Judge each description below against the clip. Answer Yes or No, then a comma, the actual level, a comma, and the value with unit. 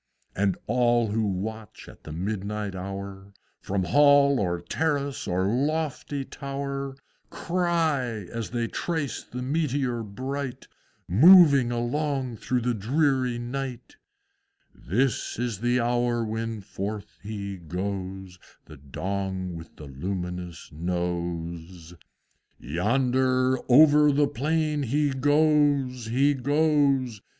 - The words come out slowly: Yes, slow, 110 wpm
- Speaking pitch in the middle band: No, low, 120 Hz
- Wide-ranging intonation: Yes, wide, 6.2 semitones